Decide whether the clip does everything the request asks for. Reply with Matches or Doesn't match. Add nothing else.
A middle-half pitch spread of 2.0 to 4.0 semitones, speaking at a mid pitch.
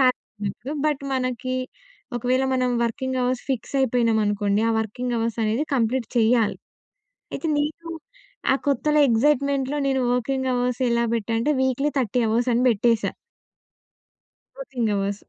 Doesn't match